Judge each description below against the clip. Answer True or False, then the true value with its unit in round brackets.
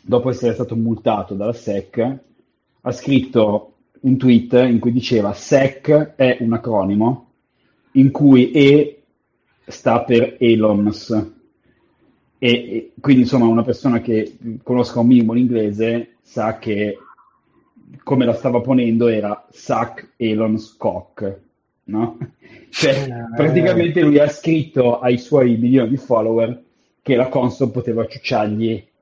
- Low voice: True (120 Hz)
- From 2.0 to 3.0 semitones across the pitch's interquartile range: True (2.6 semitones)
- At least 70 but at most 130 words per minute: True (125 wpm)